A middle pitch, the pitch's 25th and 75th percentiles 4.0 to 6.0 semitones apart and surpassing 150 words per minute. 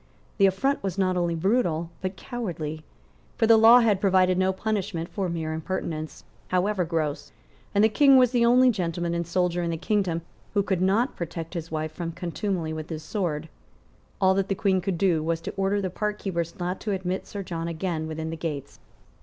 No: medium, 180 Hz; average, 3.3 semitones; average, 195 wpm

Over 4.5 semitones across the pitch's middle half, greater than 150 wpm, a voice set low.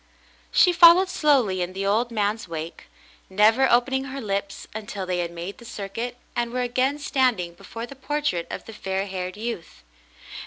No: average, 5.3 semitones; average, 180 wpm; high, 220 Hz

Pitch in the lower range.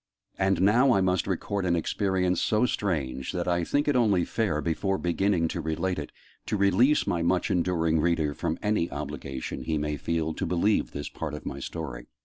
Yes: very low, 90 Hz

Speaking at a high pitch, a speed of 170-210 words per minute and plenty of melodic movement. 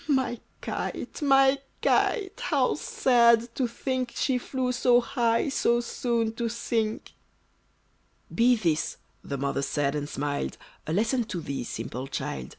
No: high, 235 Hz; average, 140 wpm; wide, 7.6 semitones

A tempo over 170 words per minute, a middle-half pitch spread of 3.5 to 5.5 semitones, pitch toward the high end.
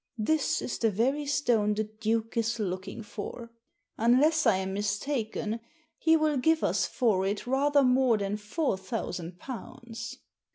No: average, 150 wpm; average, 4.3 semitones; high, 230 Hz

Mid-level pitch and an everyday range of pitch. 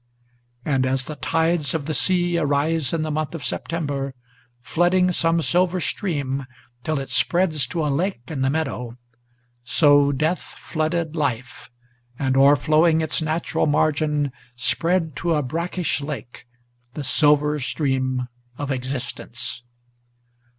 Yes: medium, 150 Hz; average, 3.4 semitones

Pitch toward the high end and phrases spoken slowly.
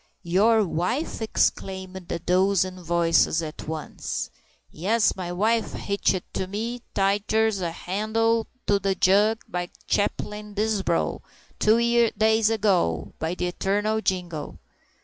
Yes: high, 195 Hz; slow, 120 wpm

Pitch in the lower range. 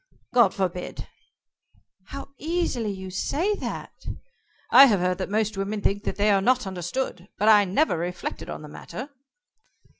No: high, 205 Hz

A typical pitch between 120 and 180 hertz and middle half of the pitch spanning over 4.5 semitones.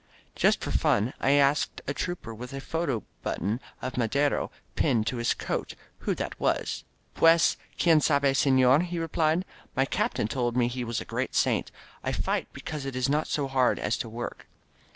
No: low, 135 Hz; average, 3.7 semitones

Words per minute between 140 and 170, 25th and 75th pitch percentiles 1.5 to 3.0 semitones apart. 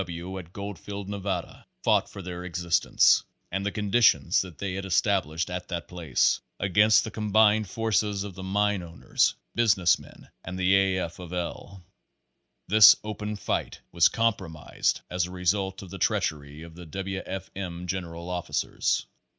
Yes: average, 160 wpm; average, 2.7 semitones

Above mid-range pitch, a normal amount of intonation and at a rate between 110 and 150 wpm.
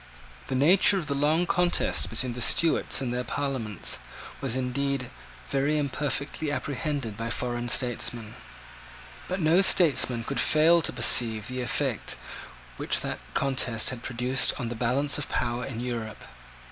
No: low, 130 Hz; average, 3.5 semitones; average, 145 wpm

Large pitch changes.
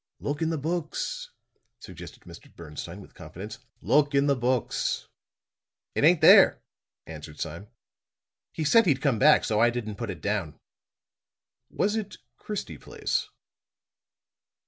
Yes: wide, 7.5 semitones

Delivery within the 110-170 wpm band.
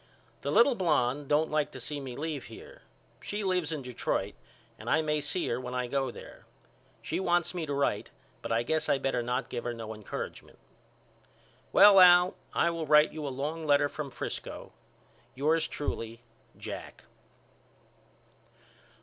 Yes: average, 165 wpm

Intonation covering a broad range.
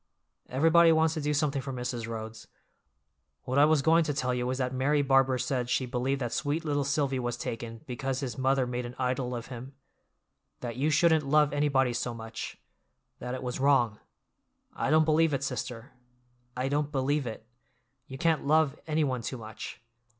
No: average, 3.1 semitones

